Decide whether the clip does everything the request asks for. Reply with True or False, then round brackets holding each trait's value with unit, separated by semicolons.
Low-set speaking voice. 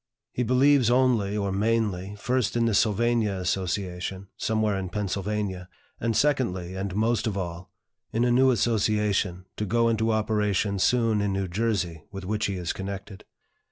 True (105 Hz)